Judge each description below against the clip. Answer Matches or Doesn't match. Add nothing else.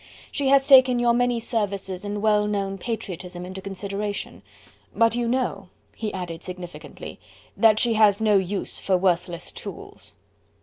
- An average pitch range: Matches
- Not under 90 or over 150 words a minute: Matches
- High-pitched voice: Matches